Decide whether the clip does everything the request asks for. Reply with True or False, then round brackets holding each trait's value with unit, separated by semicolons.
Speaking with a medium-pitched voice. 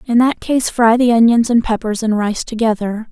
False (230 Hz)